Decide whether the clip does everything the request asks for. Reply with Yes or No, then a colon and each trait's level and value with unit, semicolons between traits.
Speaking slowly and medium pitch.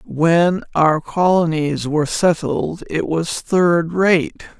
Yes: slow, 120 wpm; medium, 165 Hz